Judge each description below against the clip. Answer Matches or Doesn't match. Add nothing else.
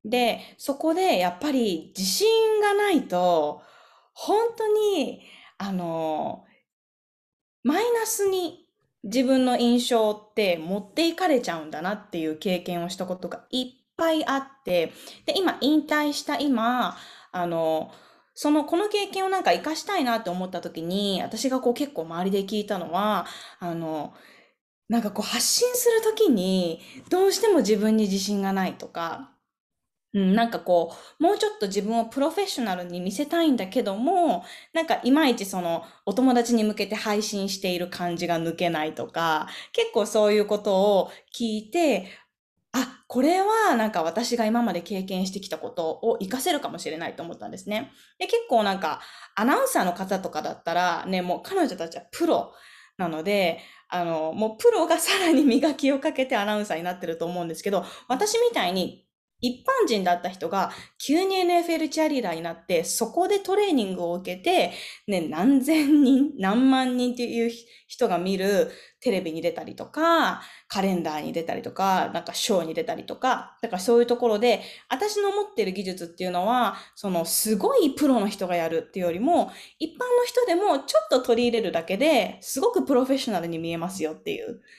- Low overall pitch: Doesn't match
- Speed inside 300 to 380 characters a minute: Matches